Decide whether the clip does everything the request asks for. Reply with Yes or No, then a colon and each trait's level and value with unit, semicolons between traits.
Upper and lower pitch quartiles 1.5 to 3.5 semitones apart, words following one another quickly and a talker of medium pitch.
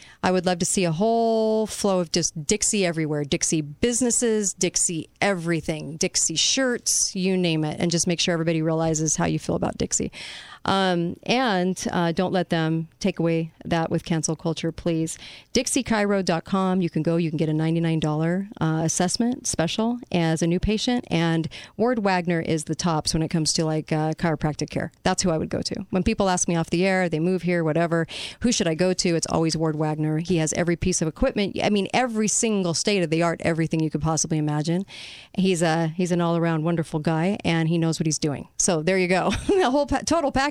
Yes: average, 3.0 semitones; fast, 215 wpm; medium, 170 Hz